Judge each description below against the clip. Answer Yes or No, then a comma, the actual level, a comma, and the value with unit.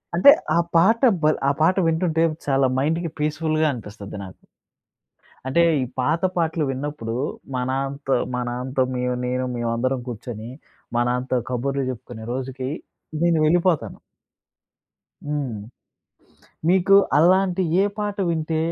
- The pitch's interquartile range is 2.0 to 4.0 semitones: No, average, 4.7 semitones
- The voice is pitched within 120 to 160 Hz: Yes, medium, 140 Hz